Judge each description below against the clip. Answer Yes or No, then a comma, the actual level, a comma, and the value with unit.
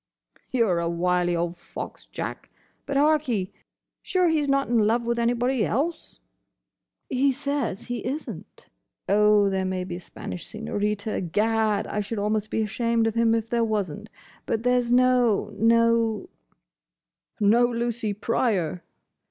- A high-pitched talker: Yes, high, 225 Hz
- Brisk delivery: No, slow, 135 wpm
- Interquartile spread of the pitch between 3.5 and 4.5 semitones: No, average, 3.1 semitones